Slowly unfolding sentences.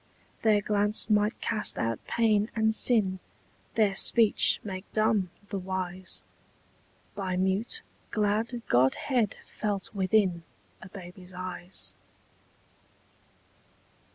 Yes: slow, 100 wpm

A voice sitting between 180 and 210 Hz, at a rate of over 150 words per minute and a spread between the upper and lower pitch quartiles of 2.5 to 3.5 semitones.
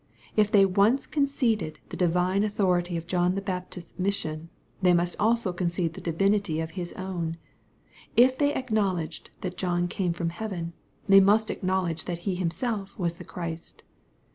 Yes: medium, 185 Hz; average, 160 wpm; average, 2.9 semitones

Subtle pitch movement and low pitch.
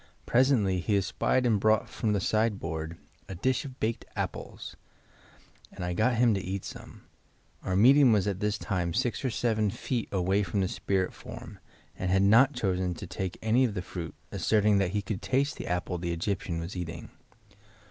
No: average, 3.8 semitones; low, 100 Hz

